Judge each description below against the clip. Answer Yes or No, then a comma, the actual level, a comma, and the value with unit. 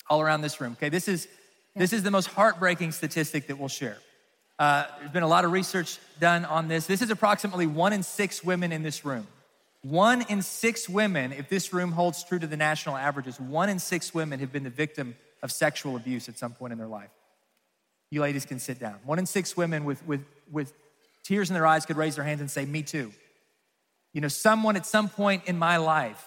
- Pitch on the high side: No, medium, 160 Hz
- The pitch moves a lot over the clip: No, average, 4.2 semitones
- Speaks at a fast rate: Yes, fast, 225 wpm